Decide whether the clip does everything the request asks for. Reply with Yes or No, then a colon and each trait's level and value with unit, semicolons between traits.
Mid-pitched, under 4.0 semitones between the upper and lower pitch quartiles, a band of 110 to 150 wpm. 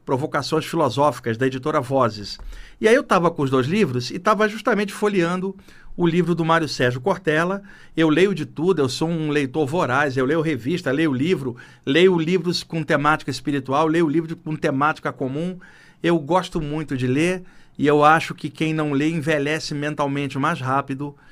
No: medium, 155 Hz; average, 3.4 semitones; average, 175 wpm